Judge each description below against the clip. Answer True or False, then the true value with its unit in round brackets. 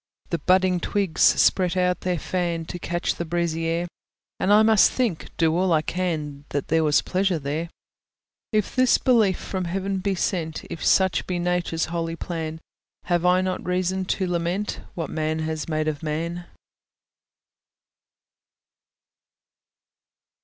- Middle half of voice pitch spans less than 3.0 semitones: True (2.4 semitones)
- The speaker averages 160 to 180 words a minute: False (145 wpm)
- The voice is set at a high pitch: False (175 Hz)